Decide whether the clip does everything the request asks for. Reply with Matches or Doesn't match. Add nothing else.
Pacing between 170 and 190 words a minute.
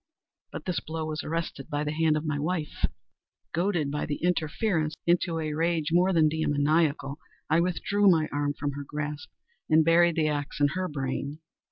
Matches